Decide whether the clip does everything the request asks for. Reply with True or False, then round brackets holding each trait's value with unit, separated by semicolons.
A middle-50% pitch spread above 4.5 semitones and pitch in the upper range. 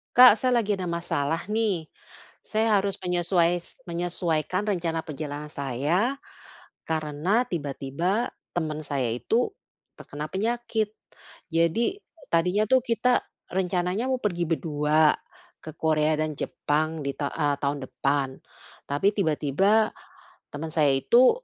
False (5.6 semitones; 170 Hz)